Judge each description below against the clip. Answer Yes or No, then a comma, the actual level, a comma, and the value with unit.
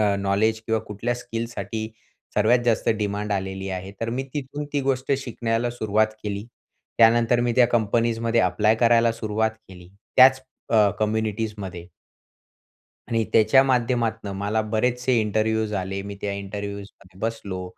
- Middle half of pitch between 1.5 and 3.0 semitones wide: Yes, narrow, 2.6 semitones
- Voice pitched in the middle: No, low, 110 Hz